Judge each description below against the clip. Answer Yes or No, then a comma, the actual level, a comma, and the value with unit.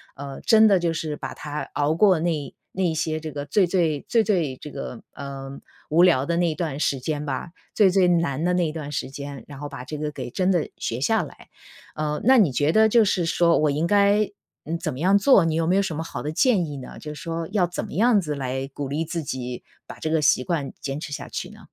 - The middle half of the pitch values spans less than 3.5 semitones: No, average, 3.9 semitones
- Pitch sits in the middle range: Yes, medium, 160 Hz